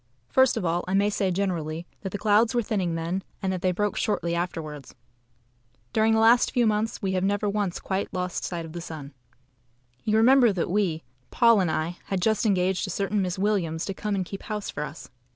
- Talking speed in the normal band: No, fast, 215 wpm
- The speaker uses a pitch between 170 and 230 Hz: Yes, high, 190 Hz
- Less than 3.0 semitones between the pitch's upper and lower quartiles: No, average, 3.4 semitones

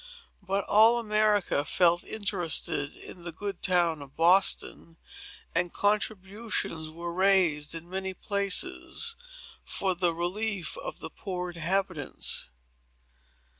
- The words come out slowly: Yes, slow, 110 wpm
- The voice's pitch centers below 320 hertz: Yes, medium, 185 Hz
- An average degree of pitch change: Yes, average, 3.1 semitones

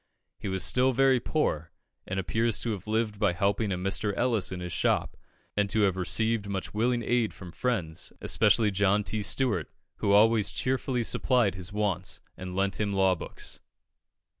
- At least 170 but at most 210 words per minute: Yes, average, 175 wpm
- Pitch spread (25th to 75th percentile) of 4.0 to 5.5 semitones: No, average, 3.4 semitones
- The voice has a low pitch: Yes, low, 105 Hz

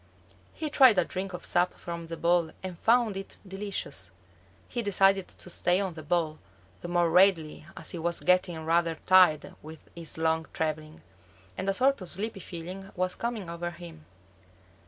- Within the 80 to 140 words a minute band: No, average, 175 wpm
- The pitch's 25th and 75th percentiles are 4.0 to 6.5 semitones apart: No, average, 3.0 semitones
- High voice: No, medium, 175 Hz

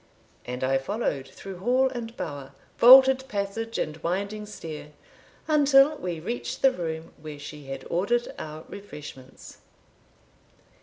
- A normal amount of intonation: No, wide, 8.3 semitones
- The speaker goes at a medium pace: No, slow, 125 wpm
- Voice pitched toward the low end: No, medium, 185 Hz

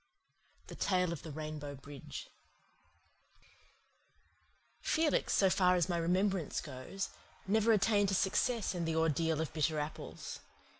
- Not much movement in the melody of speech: No, average, 3.9 semitones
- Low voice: No, medium, 170 Hz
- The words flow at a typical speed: No, slow, 130 wpm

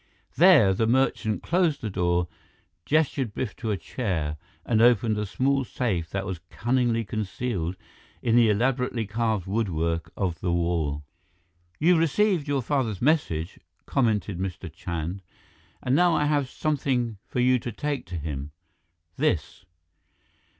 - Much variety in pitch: Yes, wide, 6.7 semitones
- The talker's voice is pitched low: Yes, low, 110 Hz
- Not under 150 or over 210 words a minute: No, average, 140 wpm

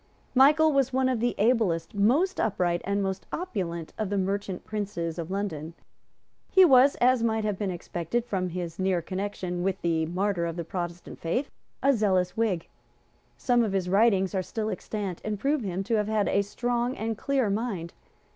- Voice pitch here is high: Yes, high, 200 Hz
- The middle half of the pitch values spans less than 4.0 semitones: No, average, 4.7 semitones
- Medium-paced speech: Yes, average, 185 wpm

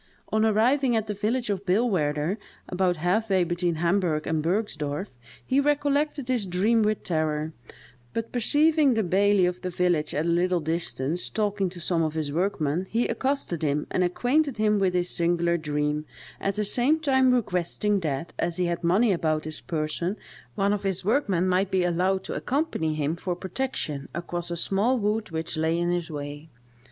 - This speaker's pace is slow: No, average, 180 wpm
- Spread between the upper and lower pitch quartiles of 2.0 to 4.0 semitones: No, average, 4.7 semitones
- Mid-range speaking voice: Yes, medium, 180 Hz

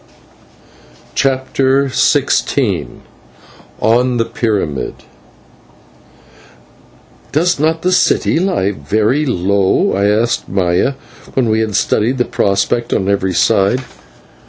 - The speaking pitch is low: Yes, low, 115 Hz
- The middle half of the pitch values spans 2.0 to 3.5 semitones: No, average, 5.0 semitones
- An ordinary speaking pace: No, slow, 105 wpm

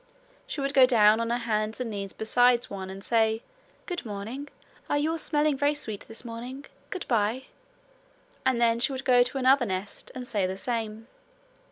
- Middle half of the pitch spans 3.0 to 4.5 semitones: Yes, average, 3.5 semitones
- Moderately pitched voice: No, high, 235 Hz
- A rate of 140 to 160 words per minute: No, average, 190 wpm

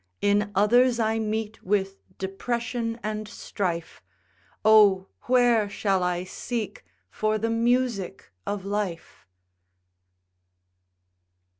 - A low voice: No, high, 210 Hz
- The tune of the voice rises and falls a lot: No, average, 2.7 semitones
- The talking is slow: Yes, slow, 95 wpm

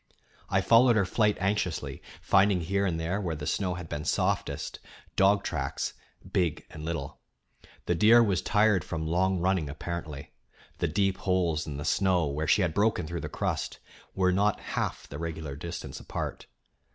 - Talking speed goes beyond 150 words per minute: Yes, average, 170 wpm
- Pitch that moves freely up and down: No, average, 3.5 semitones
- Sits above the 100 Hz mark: No, very low, 90 Hz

